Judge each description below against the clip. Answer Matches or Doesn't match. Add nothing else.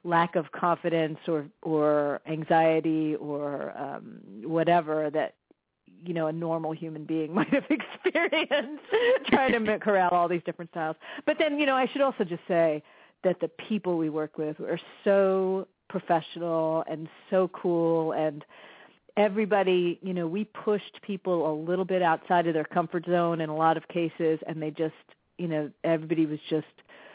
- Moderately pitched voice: Matches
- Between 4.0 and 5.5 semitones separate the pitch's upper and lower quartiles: Doesn't match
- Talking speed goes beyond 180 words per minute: Doesn't match